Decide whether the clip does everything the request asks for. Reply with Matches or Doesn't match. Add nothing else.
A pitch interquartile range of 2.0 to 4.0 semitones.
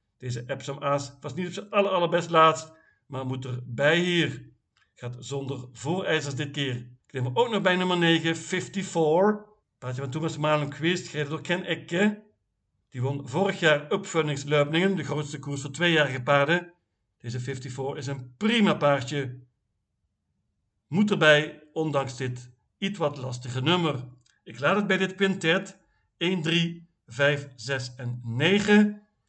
Doesn't match